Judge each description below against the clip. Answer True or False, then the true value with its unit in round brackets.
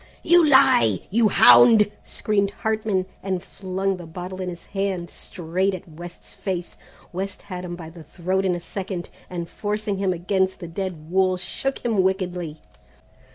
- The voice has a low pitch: False (185 Hz)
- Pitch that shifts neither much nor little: False (2.3 semitones)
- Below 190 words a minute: True (160 wpm)